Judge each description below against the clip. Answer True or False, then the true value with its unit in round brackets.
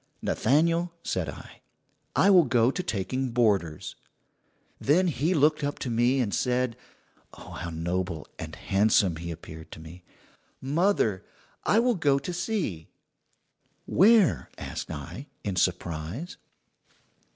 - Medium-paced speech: False (130 wpm)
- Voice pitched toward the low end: True (125 Hz)